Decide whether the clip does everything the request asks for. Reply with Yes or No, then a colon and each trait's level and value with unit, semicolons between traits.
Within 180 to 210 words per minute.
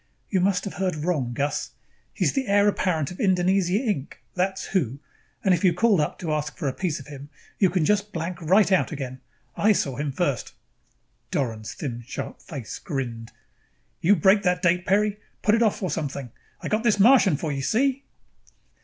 Yes: average, 190 wpm